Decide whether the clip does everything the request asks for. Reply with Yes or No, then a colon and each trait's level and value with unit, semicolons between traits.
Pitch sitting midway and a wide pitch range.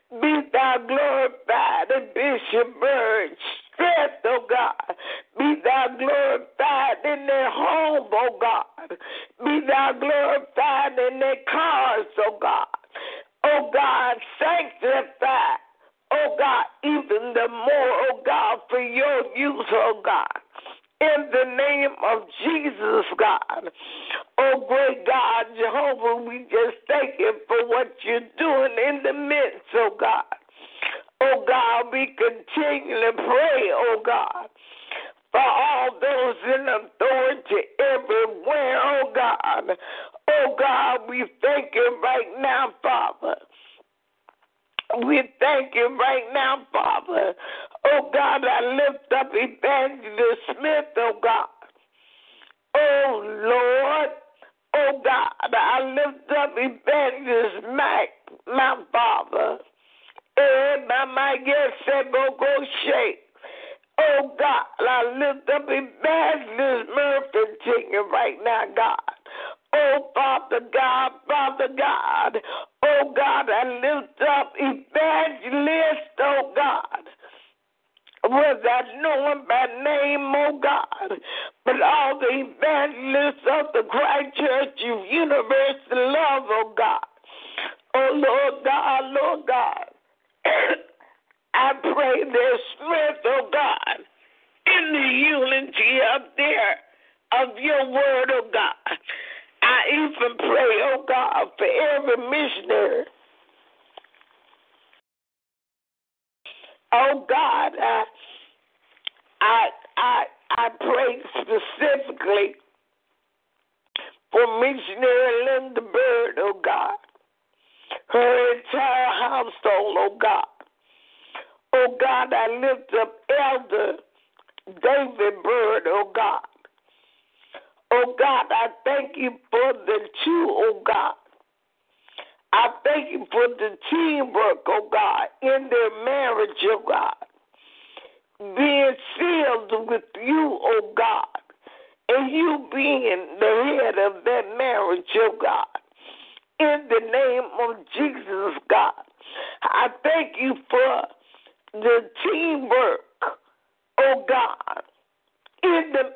No: very high, 285 Hz; wide, 7.6 semitones